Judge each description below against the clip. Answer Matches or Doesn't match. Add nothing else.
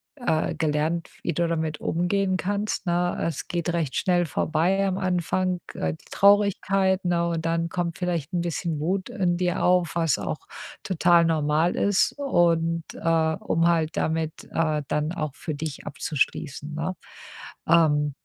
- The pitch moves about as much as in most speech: Doesn't match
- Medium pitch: Matches